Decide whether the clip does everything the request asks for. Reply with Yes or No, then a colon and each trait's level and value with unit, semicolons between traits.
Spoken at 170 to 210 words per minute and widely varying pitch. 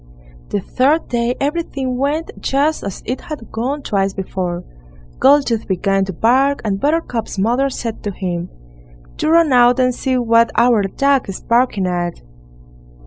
No: average, 150 wpm; wide, 5.7 semitones